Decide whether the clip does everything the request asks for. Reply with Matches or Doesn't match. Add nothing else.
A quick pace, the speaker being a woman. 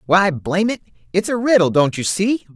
Doesn't match